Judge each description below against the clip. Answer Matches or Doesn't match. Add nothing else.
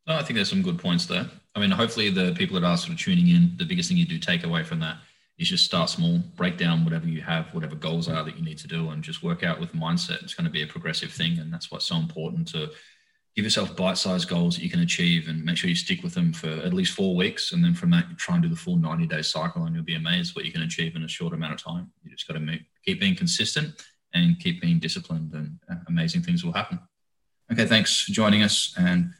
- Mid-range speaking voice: Matches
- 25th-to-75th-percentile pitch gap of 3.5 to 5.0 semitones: Doesn't match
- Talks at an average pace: Doesn't match